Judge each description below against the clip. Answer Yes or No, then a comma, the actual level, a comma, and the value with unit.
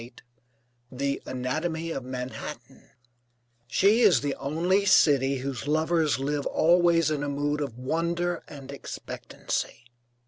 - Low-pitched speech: No, medium, 145 Hz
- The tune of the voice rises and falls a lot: No, average, 3.6 semitones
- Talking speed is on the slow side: Yes, slow, 130 wpm